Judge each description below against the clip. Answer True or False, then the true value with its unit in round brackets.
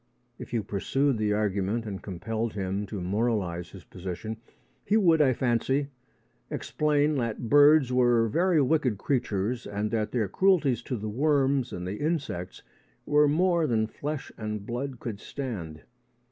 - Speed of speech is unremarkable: True (155 wpm)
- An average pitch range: False (5.7 semitones)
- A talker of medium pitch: False (115 Hz)